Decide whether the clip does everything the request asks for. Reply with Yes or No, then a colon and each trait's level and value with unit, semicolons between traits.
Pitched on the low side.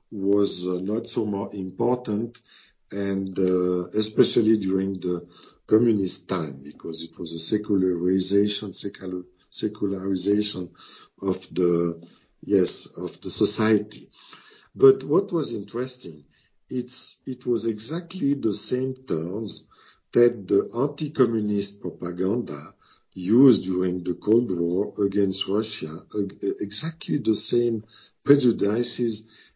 Yes: low, 105 Hz